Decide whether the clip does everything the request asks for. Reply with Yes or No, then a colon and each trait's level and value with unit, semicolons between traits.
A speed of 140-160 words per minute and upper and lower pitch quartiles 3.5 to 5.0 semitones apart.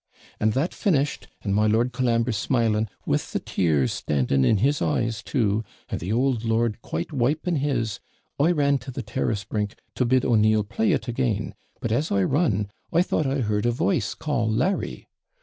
No: average, 185 wpm; average, 4.3 semitones